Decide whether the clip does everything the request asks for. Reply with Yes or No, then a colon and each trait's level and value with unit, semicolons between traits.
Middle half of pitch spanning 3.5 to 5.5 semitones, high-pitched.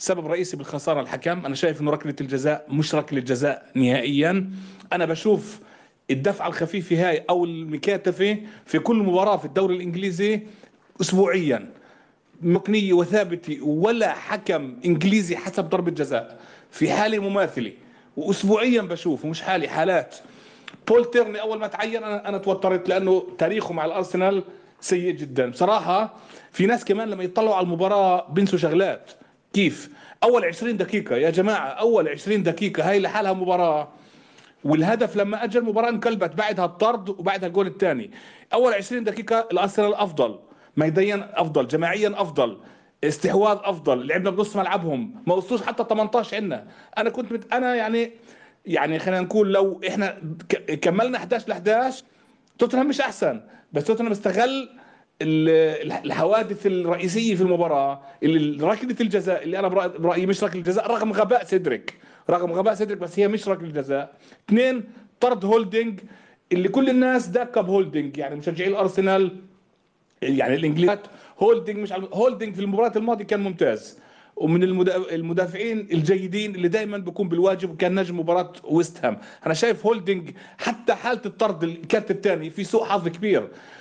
Yes: average, 4.0 semitones; high, 195 Hz